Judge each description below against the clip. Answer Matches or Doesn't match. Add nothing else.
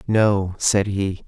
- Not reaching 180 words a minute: Matches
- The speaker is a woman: Doesn't match